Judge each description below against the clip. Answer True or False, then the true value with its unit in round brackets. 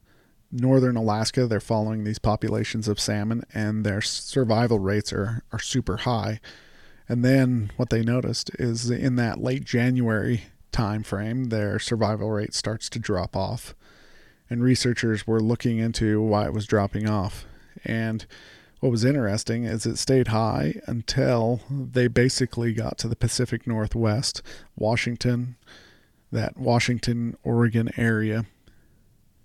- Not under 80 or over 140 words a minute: True (135 wpm)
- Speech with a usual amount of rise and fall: False (2.2 semitones)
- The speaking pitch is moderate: False (115 Hz)